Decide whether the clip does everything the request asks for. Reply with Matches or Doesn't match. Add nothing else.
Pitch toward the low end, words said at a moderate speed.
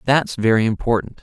Matches